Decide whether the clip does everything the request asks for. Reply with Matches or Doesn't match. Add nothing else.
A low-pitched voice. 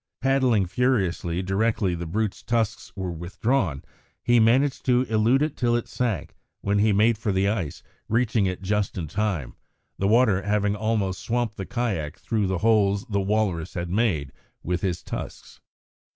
Matches